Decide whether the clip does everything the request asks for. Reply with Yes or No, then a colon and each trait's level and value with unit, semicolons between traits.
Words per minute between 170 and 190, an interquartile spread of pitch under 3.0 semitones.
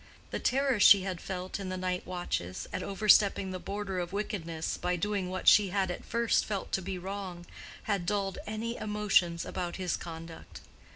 Yes: average, 180 wpm; narrow, 2.6 semitones